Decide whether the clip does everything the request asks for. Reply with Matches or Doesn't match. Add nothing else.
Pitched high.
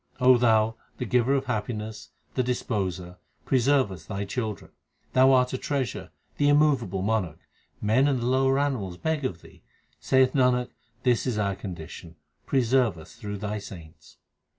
Doesn't match